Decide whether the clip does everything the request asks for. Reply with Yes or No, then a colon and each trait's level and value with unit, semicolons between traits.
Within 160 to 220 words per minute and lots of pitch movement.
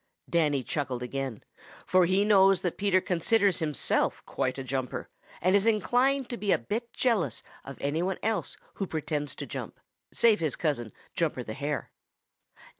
Yes: average, 165 wpm; wide, 6.5 semitones